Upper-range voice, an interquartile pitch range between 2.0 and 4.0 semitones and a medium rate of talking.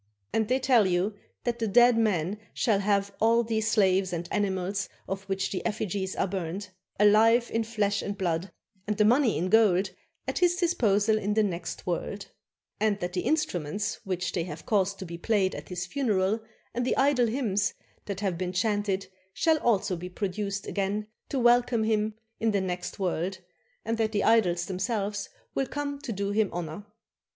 Yes: high, 205 Hz; average, 3.1 semitones; average, 180 wpm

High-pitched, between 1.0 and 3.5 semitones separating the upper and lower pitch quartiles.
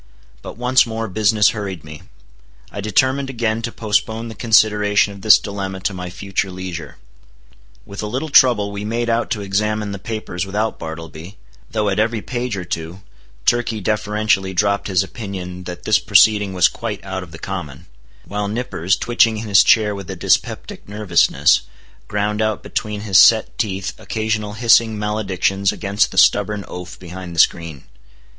No: low, 105 Hz; narrow, 2.5 semitones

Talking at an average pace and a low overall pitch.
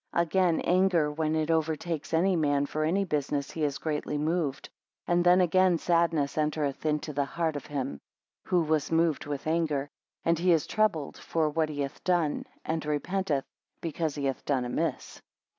No: average, 180 wpm; medium, 155 Hz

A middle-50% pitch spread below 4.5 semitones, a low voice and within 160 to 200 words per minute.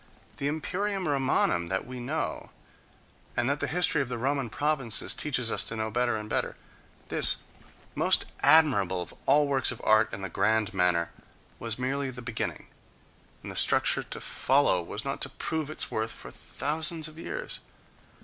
No: average, 5.2 semitones; low, 130 Hz; average, 170 wpm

